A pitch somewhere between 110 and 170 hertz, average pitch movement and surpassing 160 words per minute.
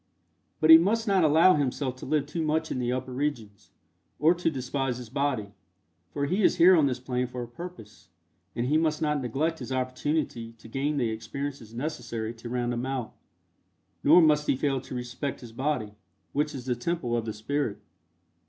Yes: low, 135 Hz; average, 3.9 semitones; average, 195 wpm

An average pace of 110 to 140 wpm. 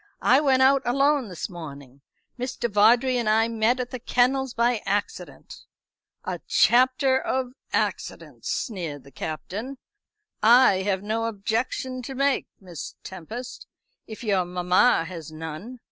Yes: slow, 135 wpm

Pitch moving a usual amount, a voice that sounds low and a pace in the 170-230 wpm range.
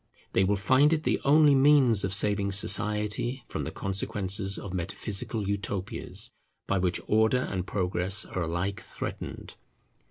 No: average, 3.0 semitones; low, 100 Hz; average, 145 wpm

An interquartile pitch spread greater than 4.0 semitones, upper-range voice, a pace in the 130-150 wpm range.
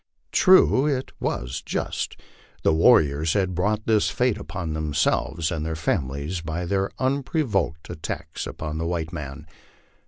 No: average, 5.2 semitones; very low, 85 Hz; average, 145 wpm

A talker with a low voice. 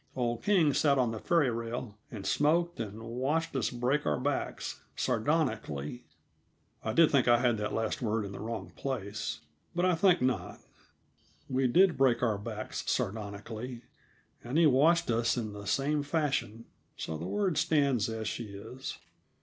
Yes: low, 125 Hz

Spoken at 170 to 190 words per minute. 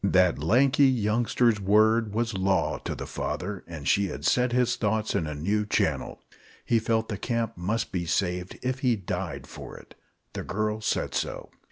Yes: average, 180 wpm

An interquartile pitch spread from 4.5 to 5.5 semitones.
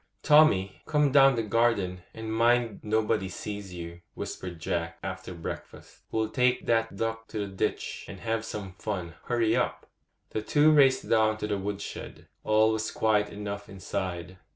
No: average, 3.1 semitones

